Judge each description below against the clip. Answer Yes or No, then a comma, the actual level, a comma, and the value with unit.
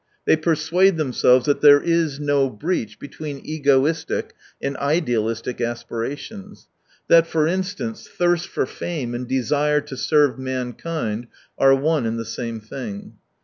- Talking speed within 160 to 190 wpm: No, average, 140 wpm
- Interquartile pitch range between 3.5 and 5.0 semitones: Yes, average, 4.5 semitones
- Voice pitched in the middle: Yes, medium, 145 Hz